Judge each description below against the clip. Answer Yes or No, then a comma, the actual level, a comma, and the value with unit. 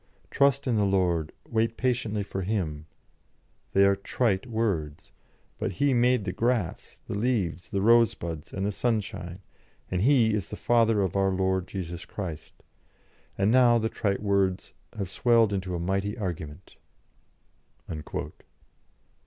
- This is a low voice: Yes, low, 100 Hz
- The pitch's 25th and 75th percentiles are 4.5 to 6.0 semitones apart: No, average, 3.8 semitones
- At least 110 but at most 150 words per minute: Yes, average, 140 wpm